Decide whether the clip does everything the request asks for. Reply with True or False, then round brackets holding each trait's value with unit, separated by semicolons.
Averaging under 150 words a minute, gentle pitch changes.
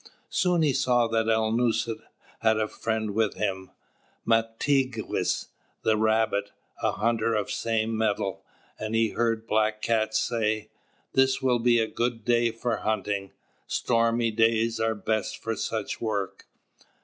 True (140 wpm; 1.2 semitones)